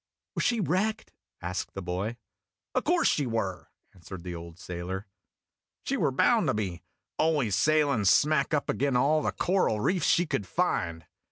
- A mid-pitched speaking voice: No, low, 110 Hz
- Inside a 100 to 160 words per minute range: No, average, 170 wpm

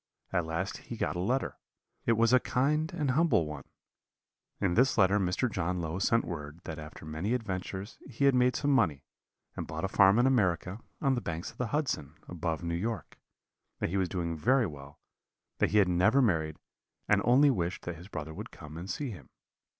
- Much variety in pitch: Yes, wide, 6.9 semitones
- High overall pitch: No, very low, 95 Hz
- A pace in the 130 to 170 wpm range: No, fast, 205 wpm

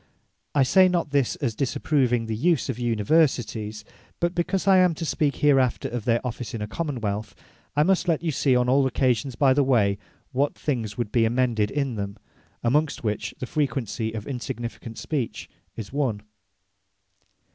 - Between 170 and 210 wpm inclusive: Yes, average, 175 wpm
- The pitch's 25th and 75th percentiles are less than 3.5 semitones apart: No, average, 4.5 semitones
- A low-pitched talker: Yes, low, 125 Hz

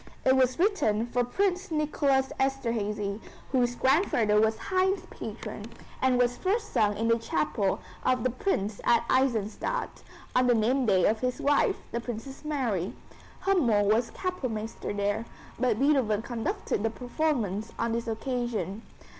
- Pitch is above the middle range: Yes, high, 240 Hz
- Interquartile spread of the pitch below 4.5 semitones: Yes, average, 3.8 semitones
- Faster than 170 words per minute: No, average, 145 wpm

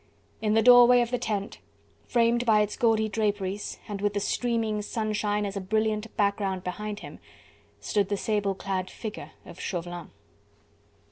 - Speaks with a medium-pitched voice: No, high, 210 Hz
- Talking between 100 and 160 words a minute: Yes, average, 155 wpm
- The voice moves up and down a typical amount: No, narrow, 1.8 semitones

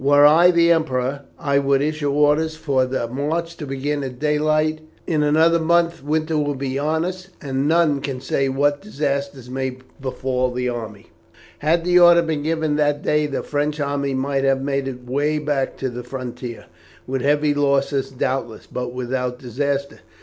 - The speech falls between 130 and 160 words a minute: No, average, 175 wpm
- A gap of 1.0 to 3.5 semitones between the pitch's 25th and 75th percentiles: Yes, narrow, 2.6 semitones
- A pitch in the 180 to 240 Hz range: No, medium, 145 Hz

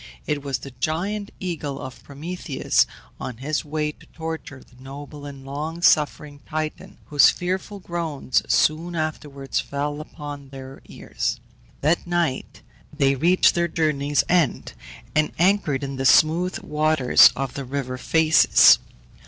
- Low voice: No, medium, 150 Hz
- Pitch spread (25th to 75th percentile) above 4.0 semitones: No, average, 2.9 semitones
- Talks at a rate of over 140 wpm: No, slow, 135 wpm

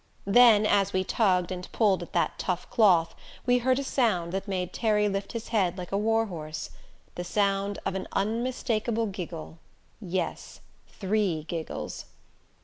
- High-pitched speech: Yes, high, 195 Hz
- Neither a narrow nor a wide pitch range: Yes, average, 3.5 semitones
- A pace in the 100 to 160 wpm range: Yes, average, 155 wpm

